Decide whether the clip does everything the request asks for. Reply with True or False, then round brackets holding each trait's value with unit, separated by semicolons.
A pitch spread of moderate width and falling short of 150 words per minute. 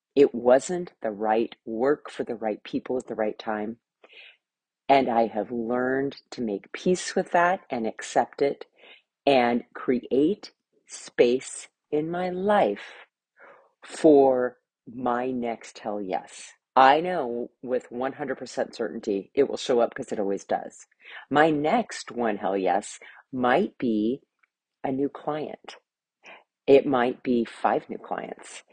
True (3.9 semitones; 135 wpm)